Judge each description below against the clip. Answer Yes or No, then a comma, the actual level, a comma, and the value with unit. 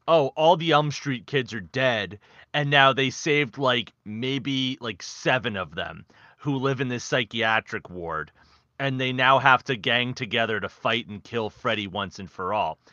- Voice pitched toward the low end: Yes, low, 130 Hz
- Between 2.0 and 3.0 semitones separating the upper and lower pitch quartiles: No, average, 3.5 semitones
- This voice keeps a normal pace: Yes, average, 185 wpm